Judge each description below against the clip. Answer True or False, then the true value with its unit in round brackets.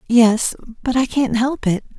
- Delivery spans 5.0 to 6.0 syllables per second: False (4.2 syllables/s)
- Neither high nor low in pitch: False (240 Hz)